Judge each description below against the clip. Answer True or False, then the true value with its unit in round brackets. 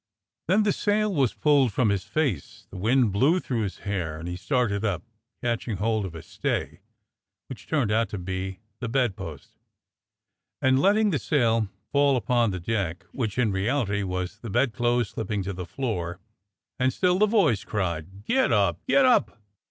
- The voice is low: True (115 Hz)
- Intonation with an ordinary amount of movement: False (5.9 semitones)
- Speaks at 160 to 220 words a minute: True (175 wpm)